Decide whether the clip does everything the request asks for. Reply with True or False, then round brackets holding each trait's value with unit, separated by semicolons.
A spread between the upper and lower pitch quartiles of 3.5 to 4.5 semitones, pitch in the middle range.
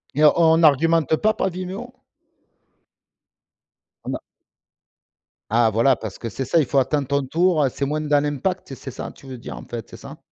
True (4.0 semitones; 145 Hz)